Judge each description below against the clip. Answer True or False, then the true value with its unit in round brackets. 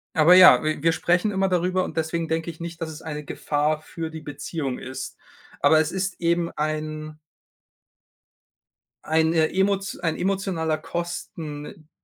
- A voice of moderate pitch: True (160 Hz)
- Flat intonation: True (2.2 semitones)